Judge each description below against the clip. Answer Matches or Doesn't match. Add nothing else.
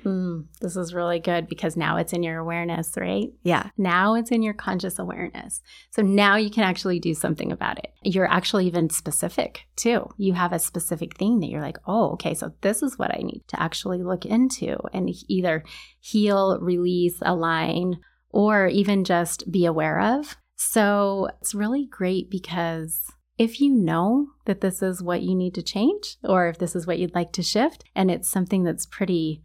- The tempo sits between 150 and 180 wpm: Doesn't match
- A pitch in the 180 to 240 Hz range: Matches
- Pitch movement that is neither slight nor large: Matches